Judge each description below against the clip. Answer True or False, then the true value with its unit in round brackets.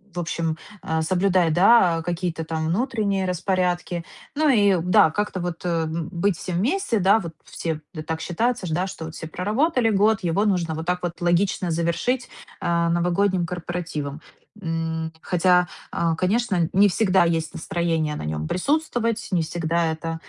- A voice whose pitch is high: False (175 Hz)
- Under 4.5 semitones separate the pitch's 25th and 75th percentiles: True (3.2 semitones)